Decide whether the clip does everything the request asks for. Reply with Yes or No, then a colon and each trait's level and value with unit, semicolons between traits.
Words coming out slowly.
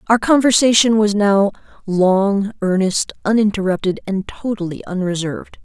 Yes: slow, 105 wpm